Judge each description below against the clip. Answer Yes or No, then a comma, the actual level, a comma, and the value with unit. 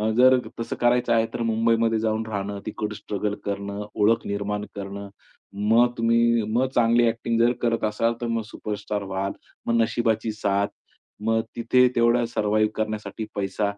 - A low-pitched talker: Yes, low, 110 Hz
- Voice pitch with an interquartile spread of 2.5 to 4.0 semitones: No, narrow, 2.1 semitones